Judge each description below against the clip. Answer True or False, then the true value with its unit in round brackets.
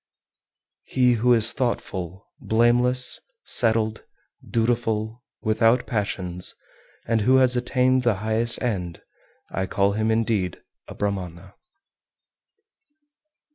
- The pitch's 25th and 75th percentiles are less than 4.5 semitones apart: True (3.2 semitones)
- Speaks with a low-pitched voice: True (110 Hz)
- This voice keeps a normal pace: False (100 wpm)